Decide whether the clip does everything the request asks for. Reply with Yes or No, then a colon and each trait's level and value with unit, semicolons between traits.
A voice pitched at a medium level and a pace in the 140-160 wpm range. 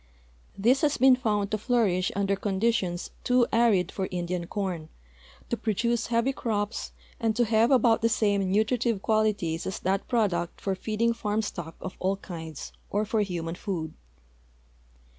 No: high, 205 Hz; average, 155 wpm